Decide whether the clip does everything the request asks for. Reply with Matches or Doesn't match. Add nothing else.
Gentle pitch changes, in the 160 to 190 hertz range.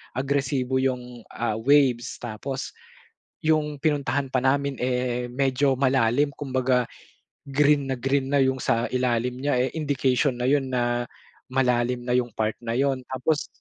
Doesn't match